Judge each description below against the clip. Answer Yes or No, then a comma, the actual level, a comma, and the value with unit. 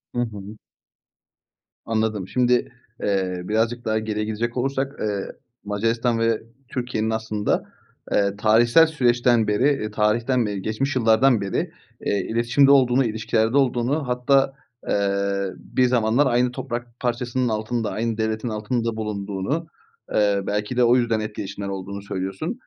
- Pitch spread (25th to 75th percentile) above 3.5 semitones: No, average, 2.8 semitones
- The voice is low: Yes, low, 115 Hz